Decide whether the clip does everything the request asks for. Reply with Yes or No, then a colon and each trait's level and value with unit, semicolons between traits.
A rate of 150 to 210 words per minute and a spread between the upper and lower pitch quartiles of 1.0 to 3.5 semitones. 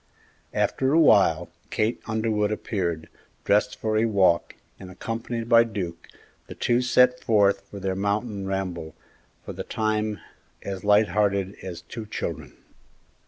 No: average, 140 wpm; average, 2.9 semitones